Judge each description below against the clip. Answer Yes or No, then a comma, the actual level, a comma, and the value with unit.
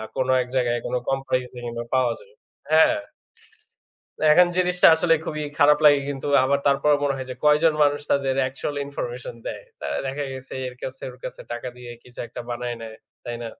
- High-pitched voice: No, low, 135 Hz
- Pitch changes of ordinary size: Yes, average, 3.0 semitones